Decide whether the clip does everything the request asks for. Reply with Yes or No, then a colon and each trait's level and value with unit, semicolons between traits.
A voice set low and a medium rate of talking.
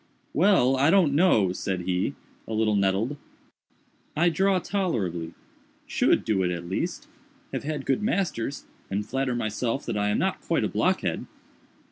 Yes: low, 125 Hz; average, 145 wpm